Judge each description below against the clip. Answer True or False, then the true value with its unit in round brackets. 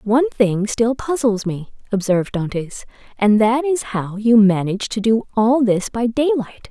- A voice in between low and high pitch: False (225 Hz)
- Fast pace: False (170 wpm)